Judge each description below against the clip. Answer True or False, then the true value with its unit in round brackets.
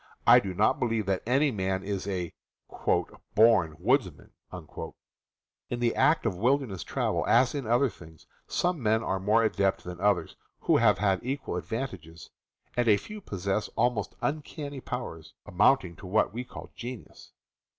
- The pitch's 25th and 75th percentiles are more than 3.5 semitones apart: True (4.7 semitones)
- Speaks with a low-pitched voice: True (110 Hz)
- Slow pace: False (160 wpm)